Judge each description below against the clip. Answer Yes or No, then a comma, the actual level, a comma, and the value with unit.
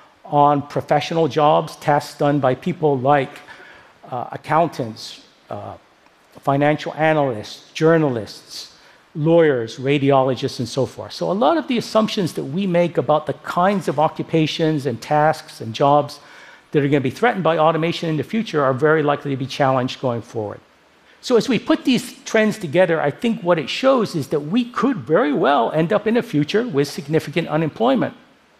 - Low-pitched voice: No, medium, 155 Hz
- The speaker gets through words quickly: No, average, 170 wpm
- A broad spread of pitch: No, average, 3.8 semitones